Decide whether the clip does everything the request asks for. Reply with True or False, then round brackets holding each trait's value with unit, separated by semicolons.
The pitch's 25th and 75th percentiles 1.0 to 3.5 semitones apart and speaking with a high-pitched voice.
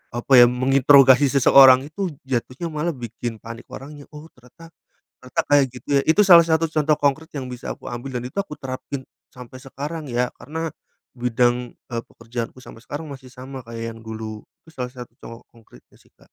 False (3.1 semitones; 130 Hz)